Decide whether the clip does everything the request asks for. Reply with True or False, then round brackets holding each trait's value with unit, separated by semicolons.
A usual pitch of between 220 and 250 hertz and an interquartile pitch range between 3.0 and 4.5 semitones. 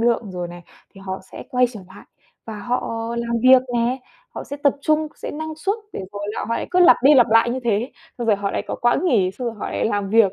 True (235 Hz; 4.2 semitones)